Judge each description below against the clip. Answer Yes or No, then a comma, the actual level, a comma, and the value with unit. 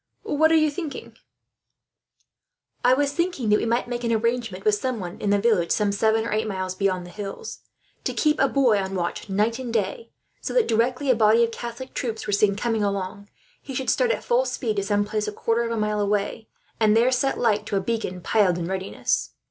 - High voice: Yes, high, 220 Hz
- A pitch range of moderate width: Yes, average, 3.6 semitones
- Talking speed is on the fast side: Yes, fast, 225 wpm